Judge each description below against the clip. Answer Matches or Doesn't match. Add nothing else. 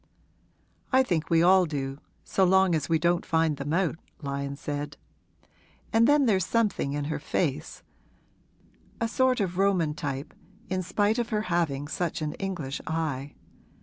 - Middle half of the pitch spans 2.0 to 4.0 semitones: Doesn't match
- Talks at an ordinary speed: Matches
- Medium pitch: Matches